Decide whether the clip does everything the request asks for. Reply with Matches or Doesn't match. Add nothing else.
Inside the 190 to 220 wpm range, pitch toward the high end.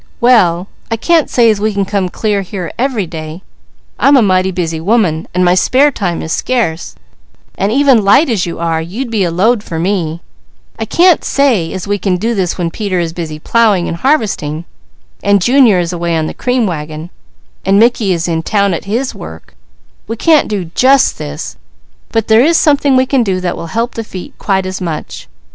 Matches